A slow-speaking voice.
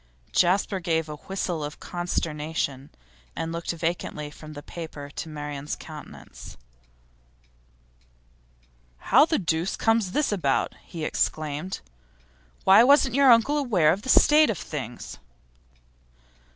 Yes: slow, 120 wpm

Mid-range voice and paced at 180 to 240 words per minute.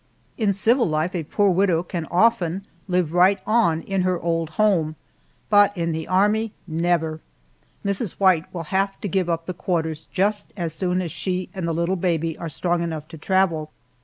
Yes: medium, 180 Hz; average, 185 wpm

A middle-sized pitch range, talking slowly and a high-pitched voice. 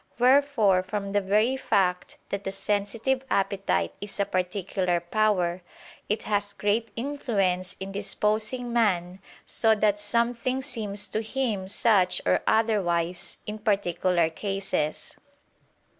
Yes: average, 3.1 semitones; slow, 120 wpm; high, 205 Hz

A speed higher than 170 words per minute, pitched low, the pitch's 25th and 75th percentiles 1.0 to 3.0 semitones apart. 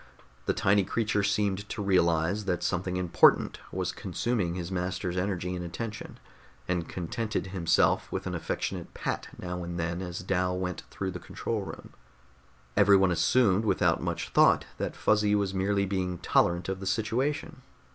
No: average, 155 wpm; very low, 95 Hz; narrow, 2.4 semitones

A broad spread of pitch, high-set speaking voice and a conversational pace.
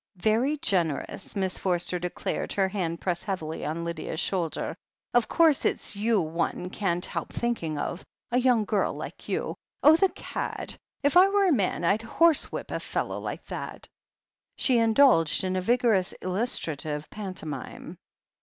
Yes: wide, 6.0 semitones; high, 195 Hz; average, 160 wpm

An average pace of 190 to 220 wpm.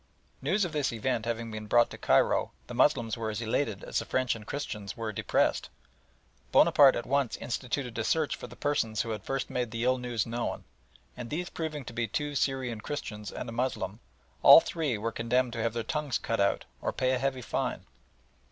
Yes: fast, 205 wpm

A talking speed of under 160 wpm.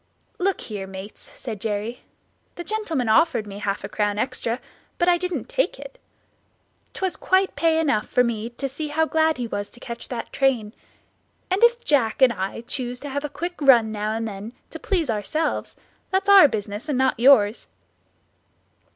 No: average, 180 wpm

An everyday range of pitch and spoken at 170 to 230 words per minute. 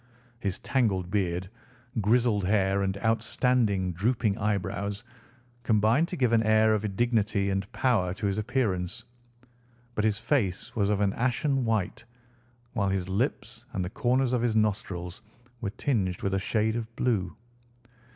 No: average, 3.5 semitones; average, 150 wpm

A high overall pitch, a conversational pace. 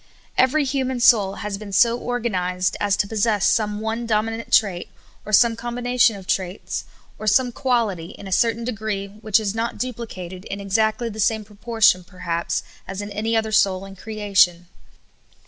Yes: high, 215 Hz; average, 170 wpm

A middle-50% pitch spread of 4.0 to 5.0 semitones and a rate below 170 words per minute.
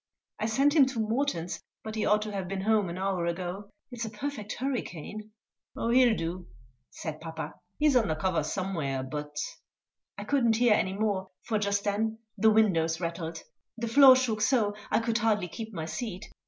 No: average, 4.6 semitones; average, 185 wpm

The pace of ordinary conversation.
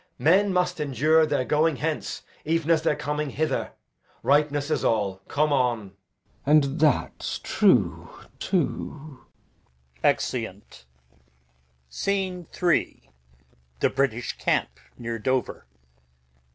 No: slow, 105 wpm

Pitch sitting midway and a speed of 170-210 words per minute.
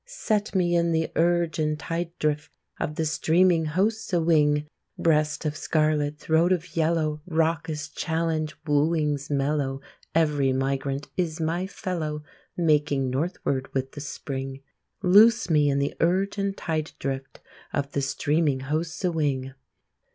No: medium, 155 Hz; average, 145 wpm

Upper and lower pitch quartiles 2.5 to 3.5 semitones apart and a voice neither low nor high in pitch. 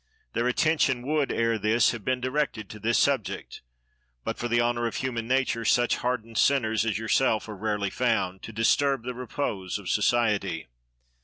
No: average, 2.8 semitones; low, 115 Hz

